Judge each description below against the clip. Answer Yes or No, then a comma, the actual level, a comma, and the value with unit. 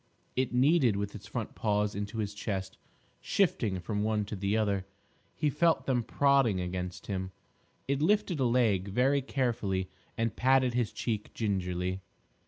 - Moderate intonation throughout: Yes, average, 4.7 semitones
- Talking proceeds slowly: No, average, 155 wpm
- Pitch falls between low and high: No, low, 110 Hz